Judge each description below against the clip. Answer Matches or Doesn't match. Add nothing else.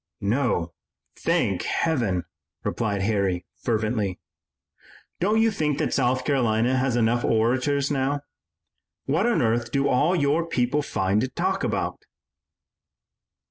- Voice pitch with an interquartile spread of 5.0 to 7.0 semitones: Doesn't match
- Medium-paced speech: Doesn't match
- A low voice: Matches